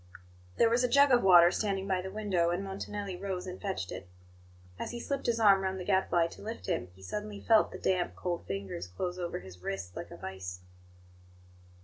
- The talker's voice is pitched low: No, high, 190 Hz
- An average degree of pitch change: Yes, average, 3.8 semitones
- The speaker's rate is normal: No, fast, 210 wpm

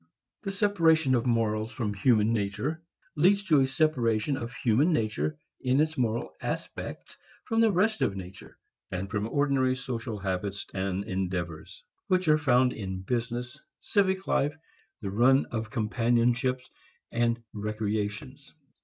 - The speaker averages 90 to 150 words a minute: Yes, slow, 135 wpm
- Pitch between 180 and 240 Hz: No, low, 120 Hz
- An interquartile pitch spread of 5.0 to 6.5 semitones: Yes, wide, 5.5 semitones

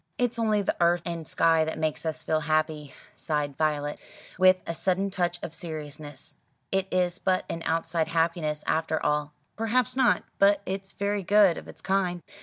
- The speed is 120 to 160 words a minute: No, average, 175 wpm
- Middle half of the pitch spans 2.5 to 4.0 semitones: Yes, average, 3.6 semitones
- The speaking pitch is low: No, medium, 170 Hz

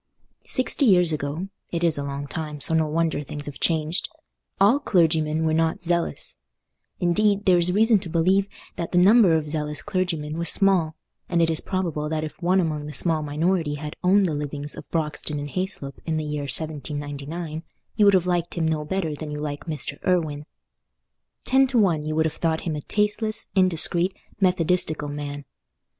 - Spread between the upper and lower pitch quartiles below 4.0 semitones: Yes, average, 3.4 semitones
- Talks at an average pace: Yes, average, 180 wpm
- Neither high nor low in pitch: Yes, medium, 160 Hz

